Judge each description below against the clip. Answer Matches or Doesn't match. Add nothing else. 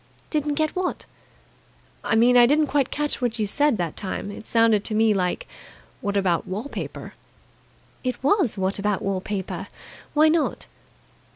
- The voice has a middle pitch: Doesn't match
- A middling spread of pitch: Doesn't match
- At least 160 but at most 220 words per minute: Matches